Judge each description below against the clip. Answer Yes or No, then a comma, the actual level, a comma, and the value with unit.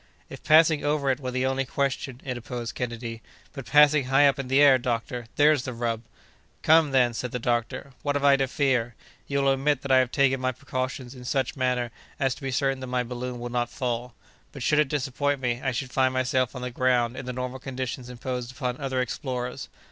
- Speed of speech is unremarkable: No, fast, 220 wpm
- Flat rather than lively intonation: Yes, narrow, 1.8 semitones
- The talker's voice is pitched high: No, low, 130 Hz